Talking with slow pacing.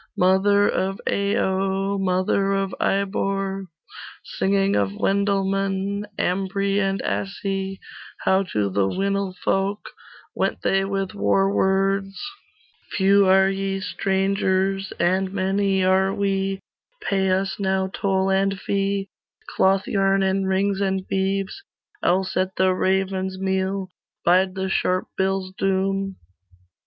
Yes: slow, 115 wpm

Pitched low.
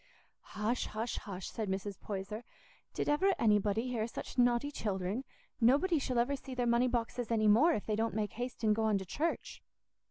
No: high, 230 Hz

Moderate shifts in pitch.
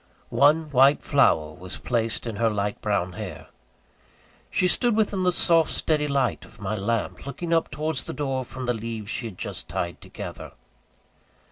No: wide, 6.2 semitones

